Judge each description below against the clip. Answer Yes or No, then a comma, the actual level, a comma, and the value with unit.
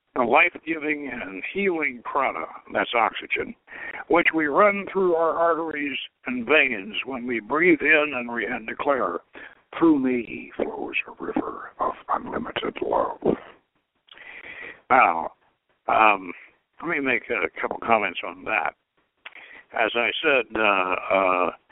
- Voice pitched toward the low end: No, medium, 165 Hz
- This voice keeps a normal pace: No, slow, 130 wpm